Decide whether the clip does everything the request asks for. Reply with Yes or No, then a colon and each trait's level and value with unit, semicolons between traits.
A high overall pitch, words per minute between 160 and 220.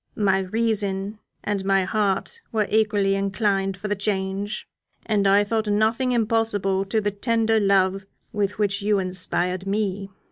No: high, 205 Hz; average, 145 wpm